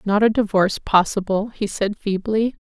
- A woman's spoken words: Yes, female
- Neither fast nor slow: Yes, average, 180 wpm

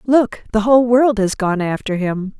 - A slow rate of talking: No, average, 200 wpm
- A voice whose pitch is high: Yes, high, 220 Hz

